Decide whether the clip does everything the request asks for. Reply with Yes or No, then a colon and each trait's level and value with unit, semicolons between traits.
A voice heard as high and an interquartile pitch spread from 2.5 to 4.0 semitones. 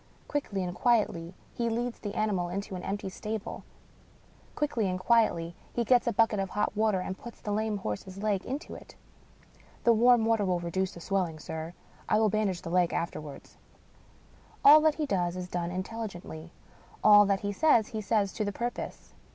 Yes: high, 205 Hz; average, 3.7 semitones